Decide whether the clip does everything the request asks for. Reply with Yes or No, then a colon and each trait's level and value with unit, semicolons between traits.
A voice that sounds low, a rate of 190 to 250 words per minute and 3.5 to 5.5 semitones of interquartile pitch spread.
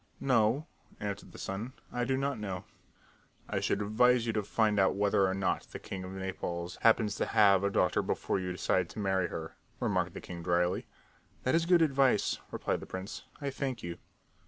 Yes: low, 100 Hz; average, 195 wpm; average, 4.7 semitones